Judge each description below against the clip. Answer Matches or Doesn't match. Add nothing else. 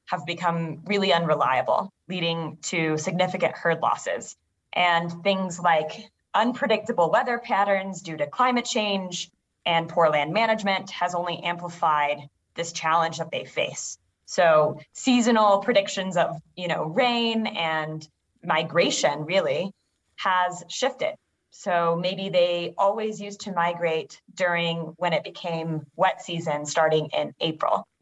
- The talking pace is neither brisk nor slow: Doesn't match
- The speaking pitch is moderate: Matches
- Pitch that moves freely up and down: Doesn't match